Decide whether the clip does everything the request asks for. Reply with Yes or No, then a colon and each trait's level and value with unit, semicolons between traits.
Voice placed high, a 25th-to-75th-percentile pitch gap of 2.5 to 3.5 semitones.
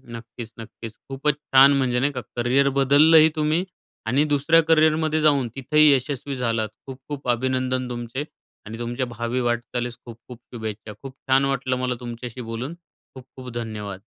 No: low, 130 Hz; average, 2.9 semitones